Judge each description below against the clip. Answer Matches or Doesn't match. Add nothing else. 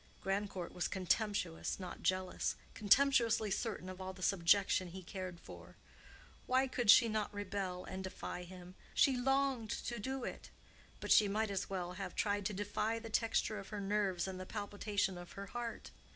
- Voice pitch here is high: Matches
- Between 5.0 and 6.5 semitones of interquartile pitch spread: Doesn't match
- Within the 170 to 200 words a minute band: Matches